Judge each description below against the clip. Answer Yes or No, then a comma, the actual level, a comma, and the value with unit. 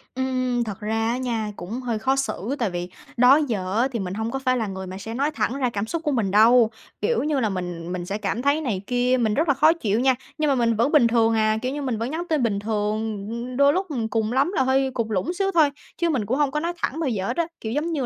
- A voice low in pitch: No, high, 240 Hz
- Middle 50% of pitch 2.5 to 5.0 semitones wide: Yes, average, 4.2 semitones